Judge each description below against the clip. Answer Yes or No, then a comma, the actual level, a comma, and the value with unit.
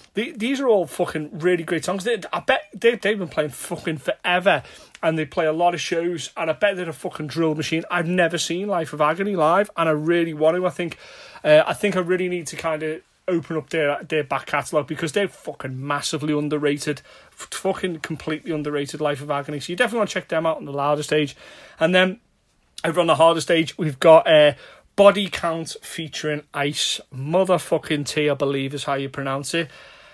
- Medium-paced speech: No, fast, 210 wpm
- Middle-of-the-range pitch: Yes, medium, 165 Hz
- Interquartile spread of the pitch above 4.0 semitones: No, average, 3.2 semitones